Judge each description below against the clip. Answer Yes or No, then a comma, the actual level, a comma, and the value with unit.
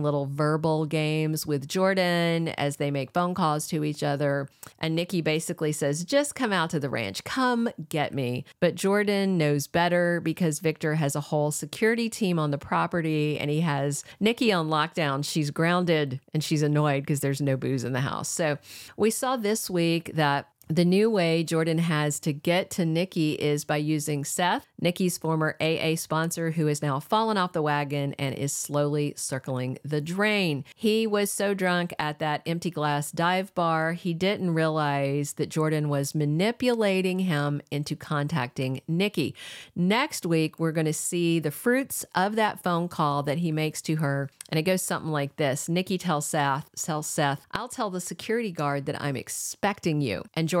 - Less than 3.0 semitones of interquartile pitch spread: No, average, 3.3 semitones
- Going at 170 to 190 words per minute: Yes, average, 185 wpm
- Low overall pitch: No, medium, 160 Hz